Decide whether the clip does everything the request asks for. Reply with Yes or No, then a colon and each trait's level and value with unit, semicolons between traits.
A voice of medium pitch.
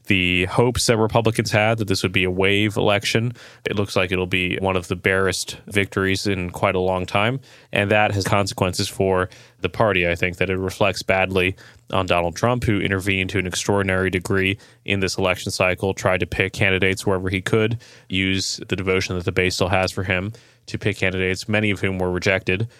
No: very low, 95 Hz